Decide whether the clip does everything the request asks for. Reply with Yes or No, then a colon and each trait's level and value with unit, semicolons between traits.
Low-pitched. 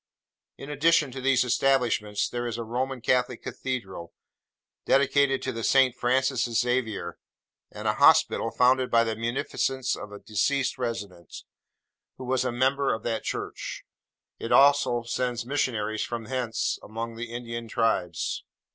Yes: low, 120 Hz